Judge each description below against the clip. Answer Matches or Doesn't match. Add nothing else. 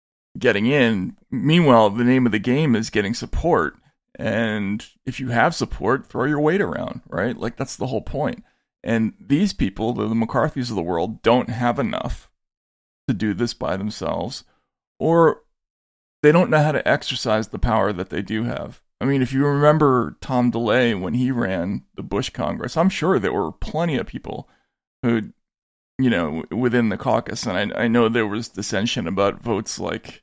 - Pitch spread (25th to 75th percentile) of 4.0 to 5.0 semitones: Doesn't match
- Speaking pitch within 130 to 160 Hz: Doesn't match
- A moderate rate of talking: Matches